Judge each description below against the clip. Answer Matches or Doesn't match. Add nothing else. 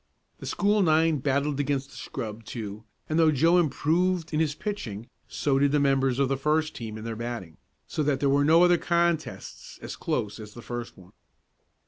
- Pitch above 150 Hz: Doesn't match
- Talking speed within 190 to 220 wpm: Matches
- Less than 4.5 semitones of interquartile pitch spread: Doesn't match